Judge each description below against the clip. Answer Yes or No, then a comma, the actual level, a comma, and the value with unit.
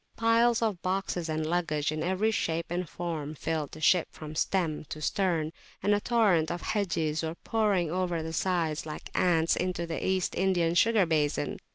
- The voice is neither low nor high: Yes, medium, 170 Hz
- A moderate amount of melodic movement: Yes, average, 3.1 semitones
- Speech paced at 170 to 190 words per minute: Yes, average, 180 wpm